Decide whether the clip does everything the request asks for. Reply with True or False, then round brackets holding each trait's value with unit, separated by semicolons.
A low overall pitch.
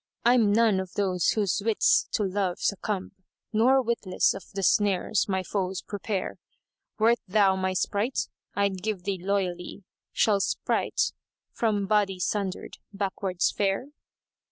False (200 Hz)